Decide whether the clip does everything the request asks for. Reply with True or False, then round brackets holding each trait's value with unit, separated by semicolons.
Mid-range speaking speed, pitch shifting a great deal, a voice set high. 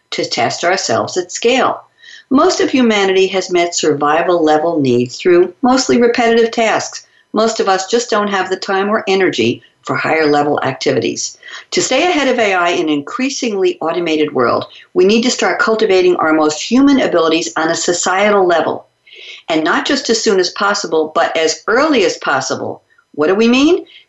True (175 wpm; 9.0 semitones; 215 Hz)